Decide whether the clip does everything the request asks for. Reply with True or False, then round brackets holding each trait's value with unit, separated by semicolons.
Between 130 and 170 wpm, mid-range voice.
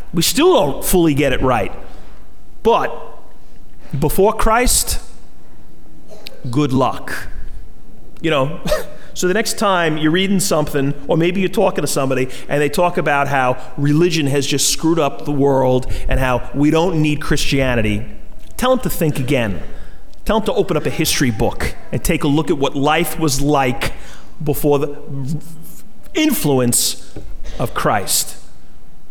True (150 wpm; 145 Hz)